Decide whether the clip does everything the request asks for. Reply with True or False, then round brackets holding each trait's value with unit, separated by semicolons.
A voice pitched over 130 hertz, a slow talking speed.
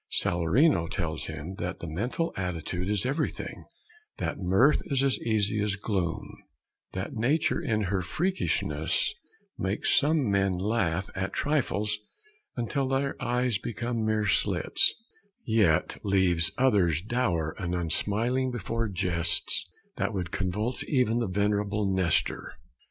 False (105 Hz; 125 wpm)